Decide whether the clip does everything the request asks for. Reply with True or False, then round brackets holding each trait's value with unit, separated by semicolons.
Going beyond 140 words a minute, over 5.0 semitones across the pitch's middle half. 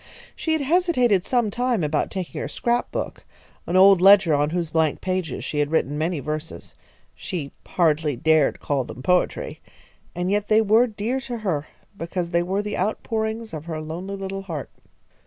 True (175 wpm; 5.4 semitones)